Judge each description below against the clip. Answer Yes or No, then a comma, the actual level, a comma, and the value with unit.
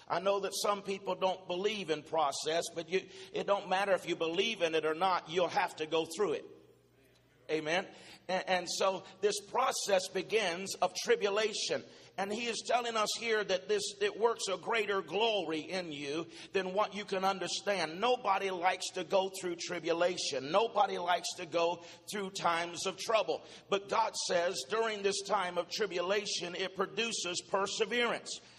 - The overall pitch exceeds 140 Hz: Yes, high, 190 Hz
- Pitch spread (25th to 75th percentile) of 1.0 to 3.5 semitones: Yes, average, 2.9 semitones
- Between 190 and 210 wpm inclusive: No, average, 170 wpm